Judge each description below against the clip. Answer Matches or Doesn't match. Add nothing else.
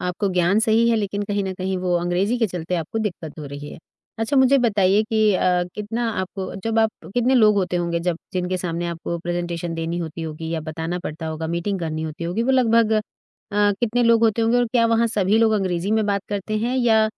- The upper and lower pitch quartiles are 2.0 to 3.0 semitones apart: Doesn't match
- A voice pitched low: Doesn't match